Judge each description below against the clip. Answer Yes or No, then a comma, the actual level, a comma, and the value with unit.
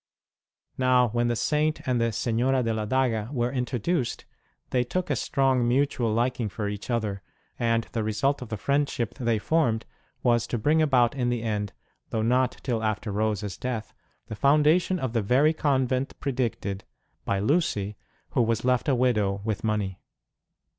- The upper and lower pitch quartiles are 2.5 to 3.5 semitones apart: Yes, average, 3.2 semitones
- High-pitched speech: No, low, 120 Hz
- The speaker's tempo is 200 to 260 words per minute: No, average, 175 wpm